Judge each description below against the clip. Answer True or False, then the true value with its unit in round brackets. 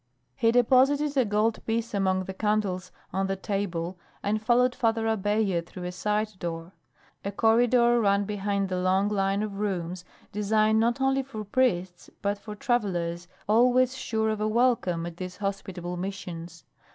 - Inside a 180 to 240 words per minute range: False (160 wpm)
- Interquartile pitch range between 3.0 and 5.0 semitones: True (3.3 semitones)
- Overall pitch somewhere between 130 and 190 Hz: False (205 Hz)